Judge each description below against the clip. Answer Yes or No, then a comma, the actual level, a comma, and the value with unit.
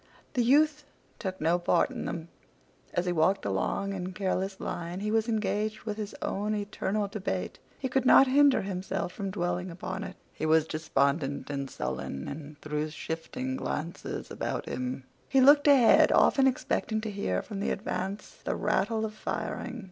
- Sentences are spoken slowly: No, average, 170 wpm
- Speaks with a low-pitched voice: No, high, 195 Hz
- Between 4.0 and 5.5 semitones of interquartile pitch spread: Yes, average, 4.7 semitones